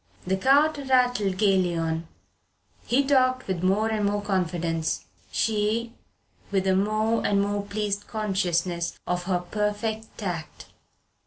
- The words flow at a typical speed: No, slow, 130 wpm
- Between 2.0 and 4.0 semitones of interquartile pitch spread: Yes, average, 3.1 semitones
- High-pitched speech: Yes, high, 205 Hz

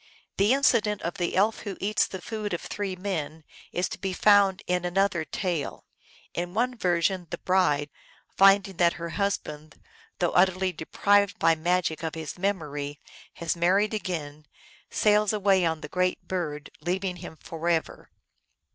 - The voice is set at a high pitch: No, medium, 180 Hz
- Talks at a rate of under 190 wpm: Yes, average, 155 wpm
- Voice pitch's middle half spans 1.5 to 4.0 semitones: Yes, average, 3.2 semitones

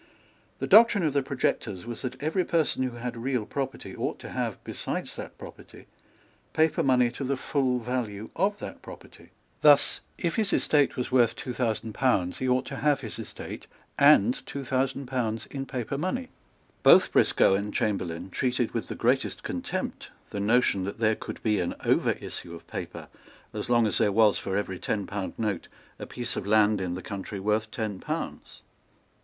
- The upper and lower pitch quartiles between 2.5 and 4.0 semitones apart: No, average, 4.5 semitones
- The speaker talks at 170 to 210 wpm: Yes, average, 185 wpm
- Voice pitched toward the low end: Yes, low, 120 Hz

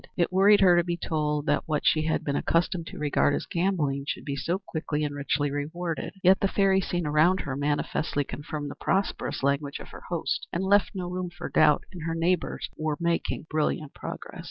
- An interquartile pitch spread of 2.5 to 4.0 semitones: Yes, average, 3.5 semitones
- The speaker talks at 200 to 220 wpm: Yes, fast, 205 wpm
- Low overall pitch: No, medium, 160 Hz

